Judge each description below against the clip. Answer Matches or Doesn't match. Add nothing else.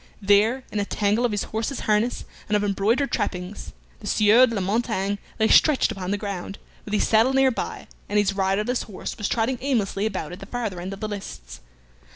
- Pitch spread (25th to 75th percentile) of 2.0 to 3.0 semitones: Matches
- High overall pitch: Matches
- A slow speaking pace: Doesn't match